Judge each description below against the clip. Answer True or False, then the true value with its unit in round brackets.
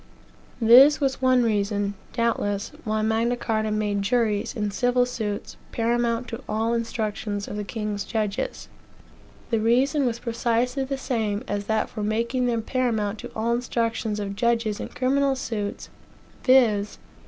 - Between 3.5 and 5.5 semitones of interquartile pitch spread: False (2.6 semitones)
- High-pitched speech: True (230 Hz)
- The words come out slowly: False (145 wpm)